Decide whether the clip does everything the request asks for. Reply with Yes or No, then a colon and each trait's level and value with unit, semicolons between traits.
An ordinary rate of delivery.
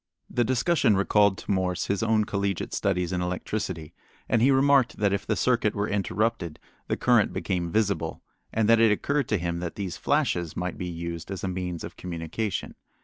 Yes: average, 190 wpm